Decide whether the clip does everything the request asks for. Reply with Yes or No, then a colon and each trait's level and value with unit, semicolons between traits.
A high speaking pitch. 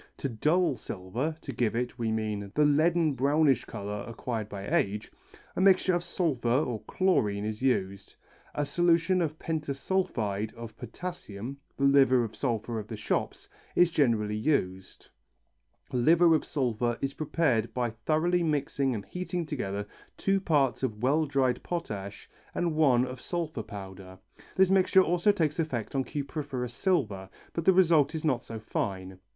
No: low, 135 Hz